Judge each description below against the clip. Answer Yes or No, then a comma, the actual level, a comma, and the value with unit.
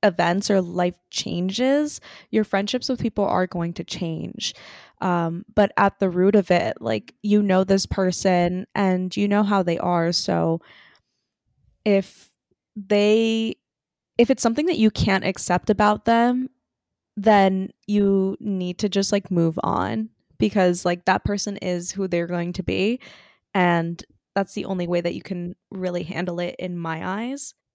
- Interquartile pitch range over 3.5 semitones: No, average, 2.9 semitones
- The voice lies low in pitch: No, high, 190 Hz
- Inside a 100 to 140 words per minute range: No, average, 160 wpm